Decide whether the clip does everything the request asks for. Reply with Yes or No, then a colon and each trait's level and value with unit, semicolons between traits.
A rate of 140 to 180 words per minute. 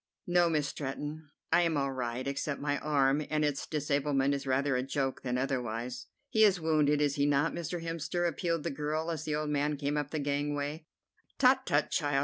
No: average, 200 wpm